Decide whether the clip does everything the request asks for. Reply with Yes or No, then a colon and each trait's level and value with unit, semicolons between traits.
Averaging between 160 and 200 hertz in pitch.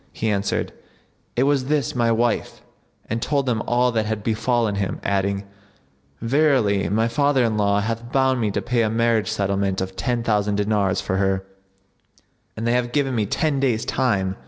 No: low, 115 Hz